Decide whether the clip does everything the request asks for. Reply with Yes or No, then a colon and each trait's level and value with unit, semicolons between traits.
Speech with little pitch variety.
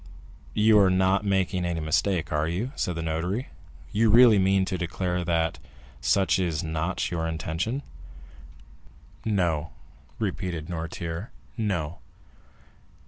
No: average, 3.2 semitones